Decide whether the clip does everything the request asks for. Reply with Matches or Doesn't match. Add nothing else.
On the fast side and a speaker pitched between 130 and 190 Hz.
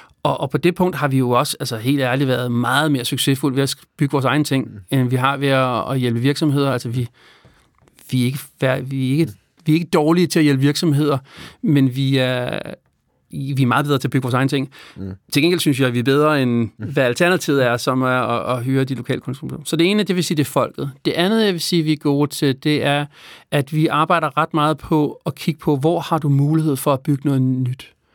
Matches